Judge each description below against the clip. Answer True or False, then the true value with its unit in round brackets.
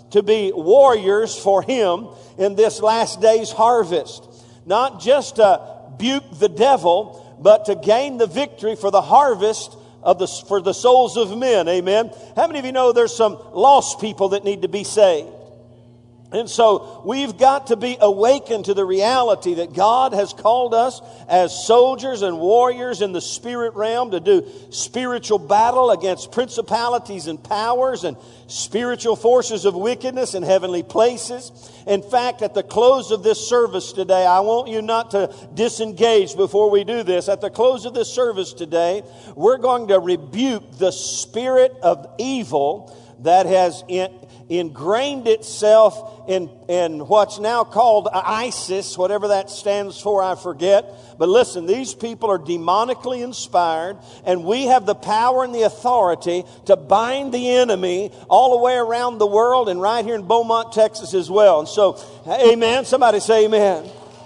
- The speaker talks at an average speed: True (165 wpm)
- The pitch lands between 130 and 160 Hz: False (215 Hz)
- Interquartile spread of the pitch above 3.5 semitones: True (4.3 semitones)